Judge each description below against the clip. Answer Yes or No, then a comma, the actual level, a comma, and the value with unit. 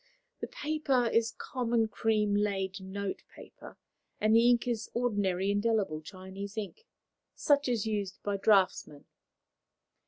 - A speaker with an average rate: No, slow, 125 wpm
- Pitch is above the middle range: Yes, high, 215 Hz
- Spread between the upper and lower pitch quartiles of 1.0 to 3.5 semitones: Yes, average, 3.1 semitones